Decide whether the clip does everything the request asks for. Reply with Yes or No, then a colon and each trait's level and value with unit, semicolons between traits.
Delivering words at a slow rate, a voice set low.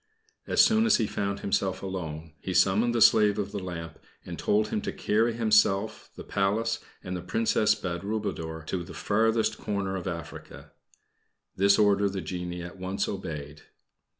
No: average, 165 wpm; low, 100 Hz